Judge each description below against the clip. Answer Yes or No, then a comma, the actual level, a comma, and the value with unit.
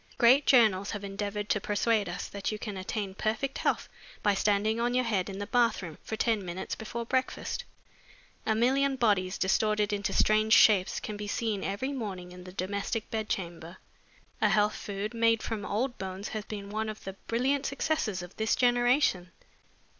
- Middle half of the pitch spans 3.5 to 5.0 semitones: No, average, 2.8 semitones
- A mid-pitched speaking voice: No, high, 210 Hz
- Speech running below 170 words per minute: No, average, 180 wpm